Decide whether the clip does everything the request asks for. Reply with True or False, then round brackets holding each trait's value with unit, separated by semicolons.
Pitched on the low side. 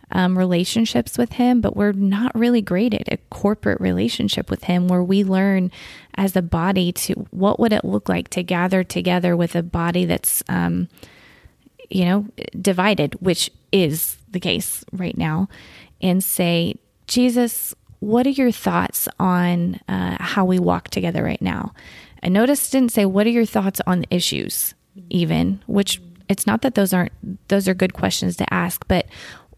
False (190 Hz)